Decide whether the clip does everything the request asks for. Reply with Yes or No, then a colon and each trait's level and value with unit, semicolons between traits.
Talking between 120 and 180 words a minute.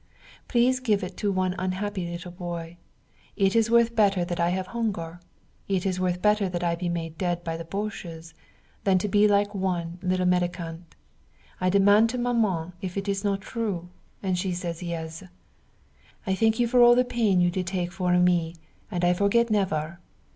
No: average, 190 wpm